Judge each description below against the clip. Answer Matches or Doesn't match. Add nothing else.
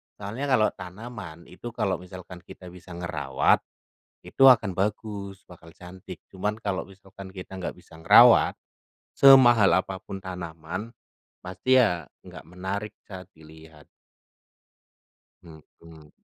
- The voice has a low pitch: Matches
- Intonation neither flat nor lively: Matches